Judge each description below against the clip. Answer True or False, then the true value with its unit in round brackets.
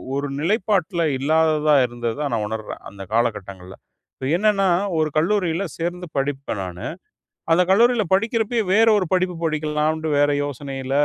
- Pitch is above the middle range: False (155 Hz)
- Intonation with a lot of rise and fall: True (6.0 semitones)